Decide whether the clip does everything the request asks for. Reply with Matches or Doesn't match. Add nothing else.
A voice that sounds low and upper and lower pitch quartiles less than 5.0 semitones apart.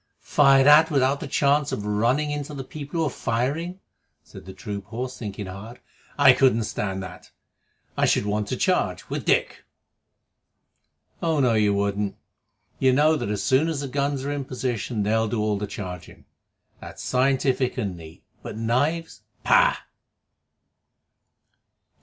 Doesn't match